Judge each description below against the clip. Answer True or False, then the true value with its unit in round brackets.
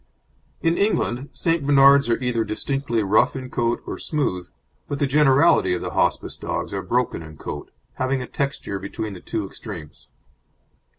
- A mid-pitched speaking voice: False (125 Hz)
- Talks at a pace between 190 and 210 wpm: False (165 wpm)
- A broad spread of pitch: False (5.0 semitones)